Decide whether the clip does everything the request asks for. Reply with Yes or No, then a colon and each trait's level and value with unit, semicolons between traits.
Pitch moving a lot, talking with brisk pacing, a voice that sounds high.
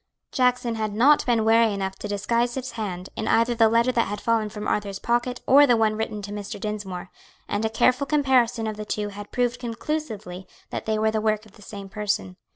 No: narrow, 2.6 semitones; fast, 220 wpm; high, 220 Hz